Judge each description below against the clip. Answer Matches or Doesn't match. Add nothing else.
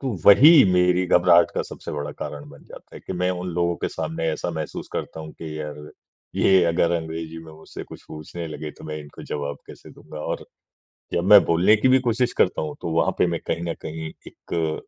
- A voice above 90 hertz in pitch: Doesn't match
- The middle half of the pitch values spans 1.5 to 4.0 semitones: Matches